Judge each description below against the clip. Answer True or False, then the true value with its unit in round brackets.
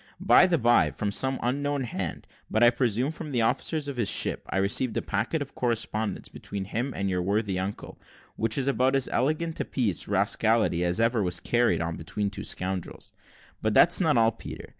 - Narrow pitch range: False (4.9 semitones)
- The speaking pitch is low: True (115 Hz)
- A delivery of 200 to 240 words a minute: True (205 wpm)